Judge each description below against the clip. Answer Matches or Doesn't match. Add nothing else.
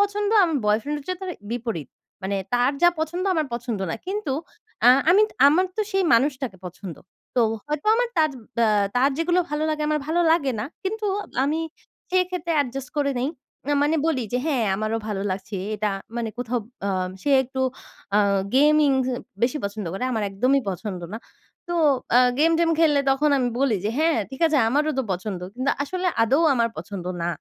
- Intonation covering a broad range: Matches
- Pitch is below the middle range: Doesn't match